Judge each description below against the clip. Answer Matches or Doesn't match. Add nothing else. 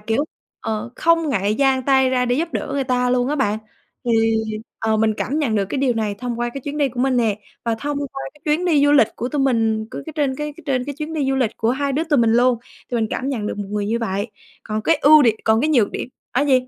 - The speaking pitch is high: Matches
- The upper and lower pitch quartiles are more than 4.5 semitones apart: Doesn't match